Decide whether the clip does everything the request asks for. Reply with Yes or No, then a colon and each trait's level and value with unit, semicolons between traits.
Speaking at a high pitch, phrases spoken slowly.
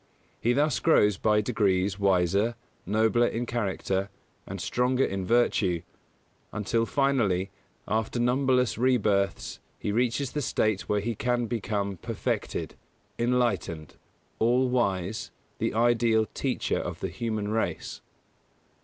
No: low, 110 Hz; slow, 120 wpm